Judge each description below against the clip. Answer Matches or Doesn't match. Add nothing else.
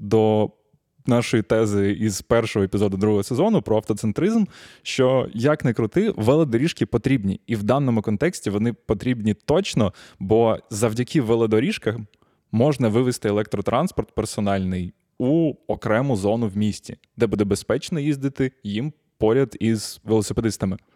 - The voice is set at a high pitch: Doesn't match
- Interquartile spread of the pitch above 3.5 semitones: Matches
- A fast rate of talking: Doesn't match